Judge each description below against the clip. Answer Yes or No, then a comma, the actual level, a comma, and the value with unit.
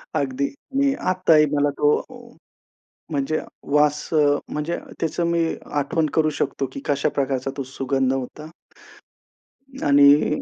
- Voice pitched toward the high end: No, medium, 150 Hz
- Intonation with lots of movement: No, narrow, 2.5 semitones